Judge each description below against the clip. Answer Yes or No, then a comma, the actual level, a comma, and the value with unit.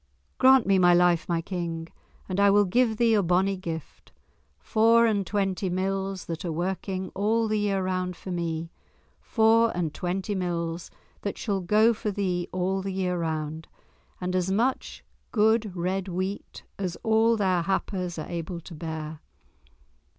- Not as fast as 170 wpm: Yes, average, 155 wpm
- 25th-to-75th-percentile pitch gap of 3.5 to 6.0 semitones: No, average, 2.8 semitones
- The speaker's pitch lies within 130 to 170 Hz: No, medium, 185 Hz